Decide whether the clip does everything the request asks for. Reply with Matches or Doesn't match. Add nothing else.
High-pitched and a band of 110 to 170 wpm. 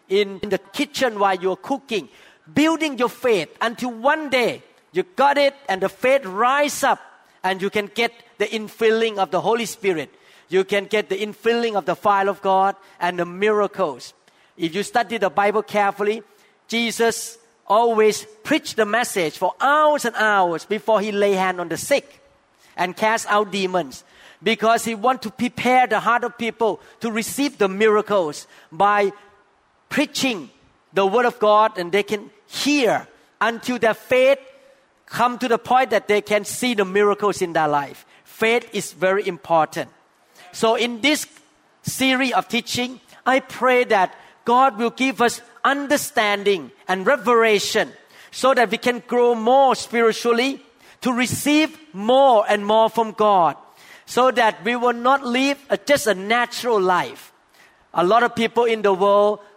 Matches